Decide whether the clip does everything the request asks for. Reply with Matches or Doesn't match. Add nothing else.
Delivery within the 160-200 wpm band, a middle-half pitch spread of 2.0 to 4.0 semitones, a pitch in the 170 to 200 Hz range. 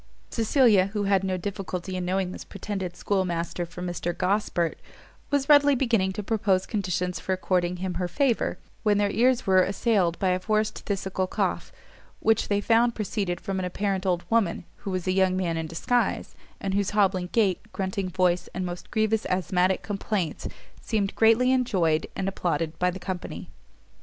Matches